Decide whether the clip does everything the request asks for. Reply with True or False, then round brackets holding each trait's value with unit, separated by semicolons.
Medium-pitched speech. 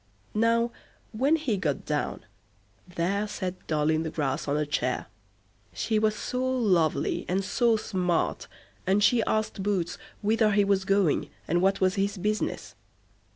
False (195 Hz)